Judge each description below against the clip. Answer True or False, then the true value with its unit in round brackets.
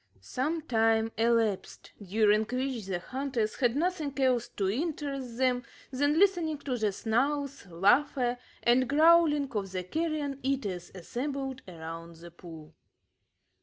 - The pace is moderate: False (130 wpm)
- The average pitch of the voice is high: True (250 Hz)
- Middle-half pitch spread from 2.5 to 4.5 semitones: False (5.5 semitones)